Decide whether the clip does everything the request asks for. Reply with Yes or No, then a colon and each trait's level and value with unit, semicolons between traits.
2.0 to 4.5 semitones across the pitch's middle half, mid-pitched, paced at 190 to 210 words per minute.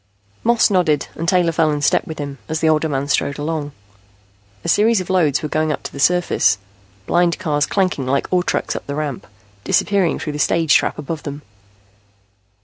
Yes: average, 3.4 semitones; medium, 155 Hz; average, 195 wpm